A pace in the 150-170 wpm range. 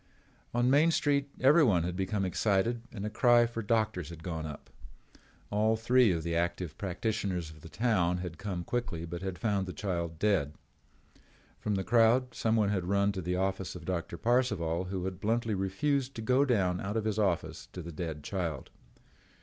No: average, 185 wpm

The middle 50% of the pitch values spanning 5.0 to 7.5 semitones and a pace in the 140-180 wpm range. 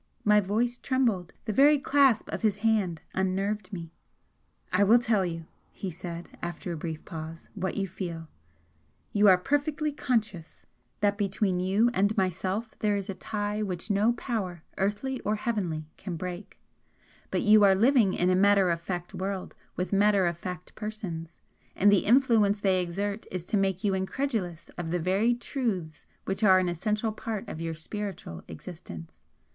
No: average, 3.4 semitones; average, 170 wpm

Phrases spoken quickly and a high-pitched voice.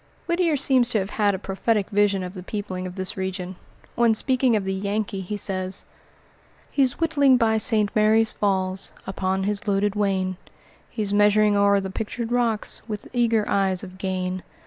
No: average, 170 wpm; high, 205 Hz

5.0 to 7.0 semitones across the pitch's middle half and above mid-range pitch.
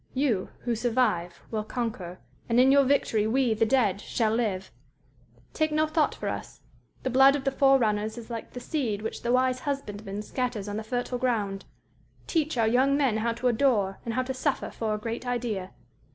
No: average, 3.5 semitones; high, 235 Hz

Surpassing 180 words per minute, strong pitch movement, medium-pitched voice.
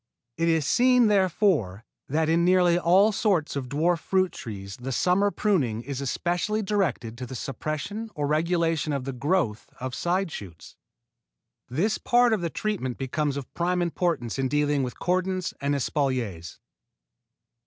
No: average, 155 wpm; wide, 5.9 semitones; medium, 160 Hz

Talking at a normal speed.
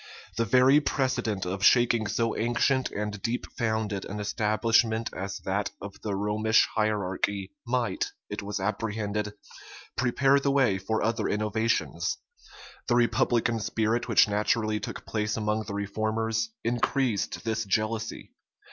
No: slow, 130 wpm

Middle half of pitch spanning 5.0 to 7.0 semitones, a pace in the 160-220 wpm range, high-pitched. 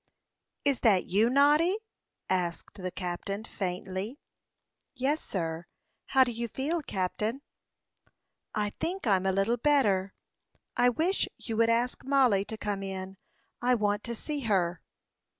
No: wide, 5.6 semitones; slow, 135 wpm; high, 220 Hz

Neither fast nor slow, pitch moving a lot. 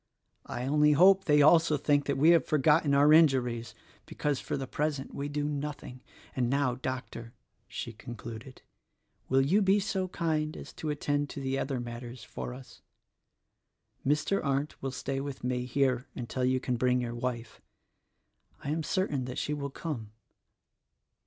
No: average, 165 wpm; average, 2.9 semitones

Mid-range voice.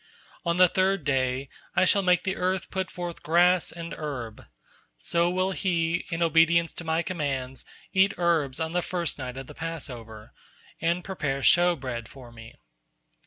Yes: medium, 165 Hz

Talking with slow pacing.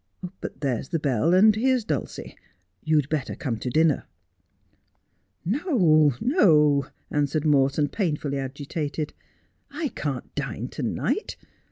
Yes: slow, 130 wpm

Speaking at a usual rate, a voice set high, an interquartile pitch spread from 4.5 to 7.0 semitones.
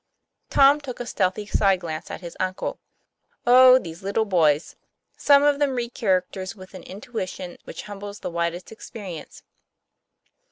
Yes: average, 150 wpm; high, 200 Hz; average, 5.0 semitones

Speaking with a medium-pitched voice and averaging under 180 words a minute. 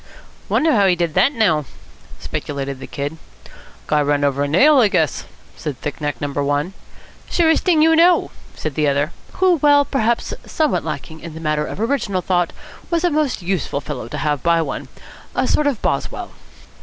No: medium, 170 Hz; average, 185 wpm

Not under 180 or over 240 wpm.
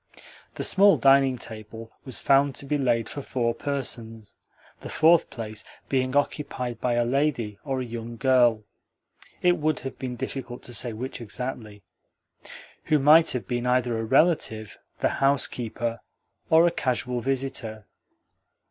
No: average, 150 wpm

